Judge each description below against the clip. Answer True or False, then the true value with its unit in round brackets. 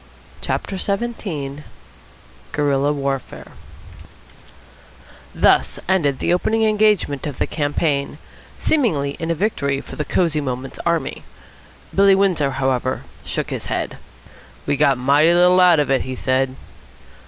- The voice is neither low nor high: True (150 Hz)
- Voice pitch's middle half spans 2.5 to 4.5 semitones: False (4.9 semitones)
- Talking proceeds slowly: True (125 wpm)